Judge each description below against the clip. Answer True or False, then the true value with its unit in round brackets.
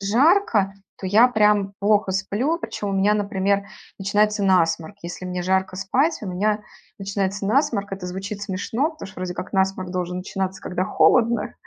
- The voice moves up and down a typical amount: False (1.9 semitones)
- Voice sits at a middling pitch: False (200 Hz)